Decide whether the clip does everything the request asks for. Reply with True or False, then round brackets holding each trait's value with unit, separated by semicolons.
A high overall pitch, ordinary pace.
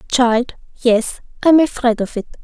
True (245 Hz; 150 wpm)